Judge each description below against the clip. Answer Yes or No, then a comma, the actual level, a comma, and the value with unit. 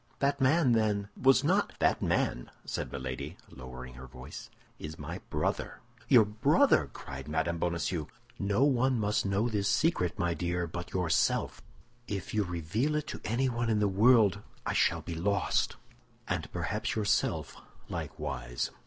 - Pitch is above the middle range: No, low, 100 Hz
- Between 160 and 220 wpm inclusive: No, average, 150 wpm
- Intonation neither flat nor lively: No, wide, 6.5 semitones